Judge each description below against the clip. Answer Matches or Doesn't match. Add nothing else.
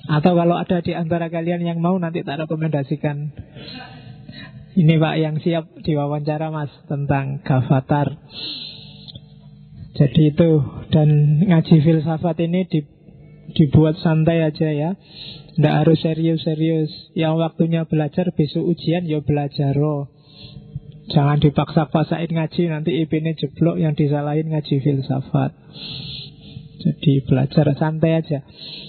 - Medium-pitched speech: Matches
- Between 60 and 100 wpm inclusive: Doesn't match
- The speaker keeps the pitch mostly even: Matches